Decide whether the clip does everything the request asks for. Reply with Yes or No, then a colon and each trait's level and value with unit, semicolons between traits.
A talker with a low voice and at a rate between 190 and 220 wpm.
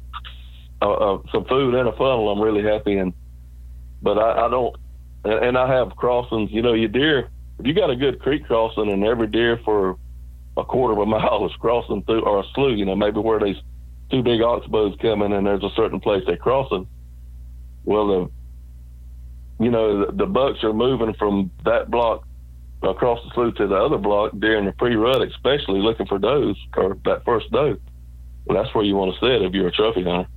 Yes: very low, 95 Hz; fast, 205 wpm